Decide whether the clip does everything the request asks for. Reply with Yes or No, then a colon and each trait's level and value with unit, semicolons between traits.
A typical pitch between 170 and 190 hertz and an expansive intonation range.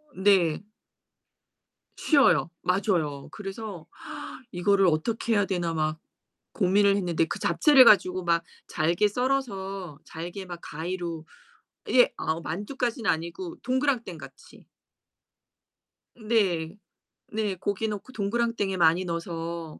No: medium, 185 Hz; average, 4.0 semitones